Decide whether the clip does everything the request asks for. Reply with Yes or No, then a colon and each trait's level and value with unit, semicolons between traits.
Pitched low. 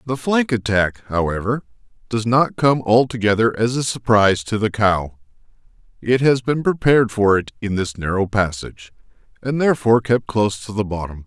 Yes: low, 110 Hz